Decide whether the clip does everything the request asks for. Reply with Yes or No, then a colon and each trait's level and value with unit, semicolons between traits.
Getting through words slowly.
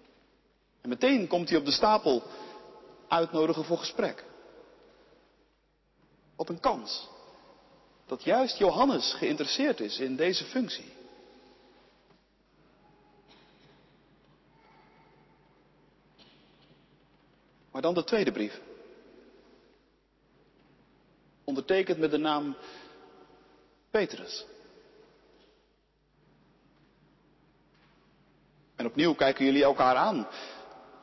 Yes: slow, 70 wpm